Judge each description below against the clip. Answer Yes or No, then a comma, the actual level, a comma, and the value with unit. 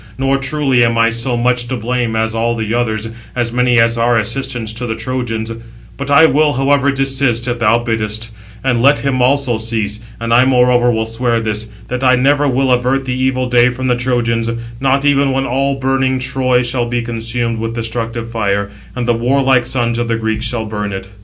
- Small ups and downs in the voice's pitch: Yes, narrow, 2.3 semitones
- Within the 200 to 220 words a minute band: Yes, fast, 205 wpm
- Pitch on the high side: No, low, 120 Hz